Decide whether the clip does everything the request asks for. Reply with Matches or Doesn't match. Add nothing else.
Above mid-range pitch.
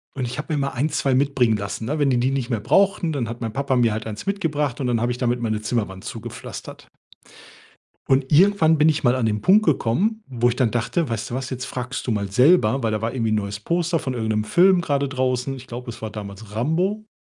Doesn't match